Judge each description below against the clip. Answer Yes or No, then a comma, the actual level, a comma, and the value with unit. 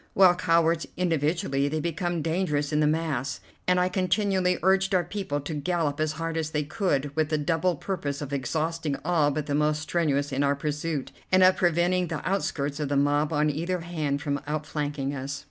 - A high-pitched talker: No, medium, 155 Hz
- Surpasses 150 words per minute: Yes, average, 195 wpm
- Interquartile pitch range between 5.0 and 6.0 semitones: No, average, 3.2 semitones